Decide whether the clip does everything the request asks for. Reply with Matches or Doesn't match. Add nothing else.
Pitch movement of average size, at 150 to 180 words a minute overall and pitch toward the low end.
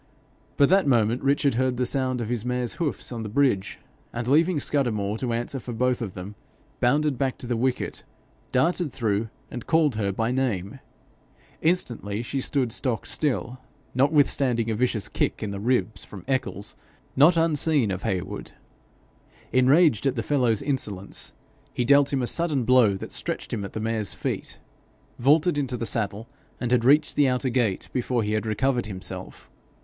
Matches